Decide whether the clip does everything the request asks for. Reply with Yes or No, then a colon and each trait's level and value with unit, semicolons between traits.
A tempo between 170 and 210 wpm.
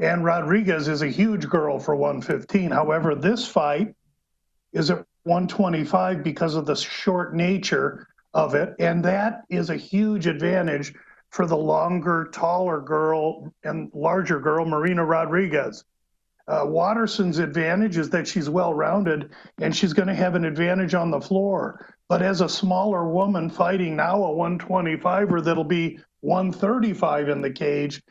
No: average, 150 wpm